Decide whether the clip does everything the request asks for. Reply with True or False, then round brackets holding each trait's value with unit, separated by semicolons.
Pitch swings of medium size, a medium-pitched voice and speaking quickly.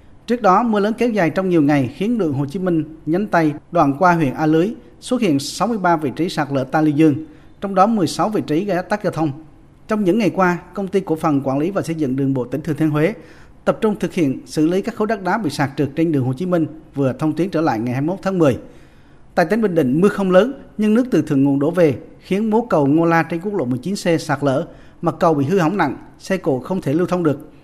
True (4.2 semitones; 165 Hz; 270 wpm)